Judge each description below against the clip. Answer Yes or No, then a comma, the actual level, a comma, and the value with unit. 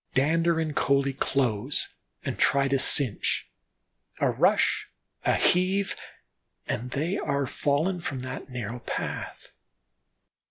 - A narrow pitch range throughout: No, average, 3.9 semitones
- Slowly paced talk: Yes, slow, 115 wpm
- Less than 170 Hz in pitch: Yes, medium, 140 Hz